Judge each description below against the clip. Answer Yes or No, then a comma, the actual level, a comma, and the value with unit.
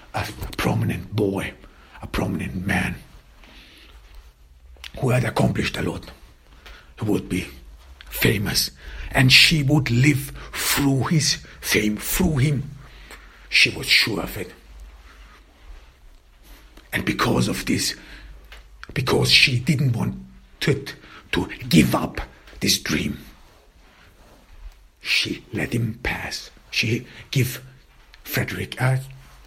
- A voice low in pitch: Yes, very low, 95 Hz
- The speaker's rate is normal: No, slow, 105 wpm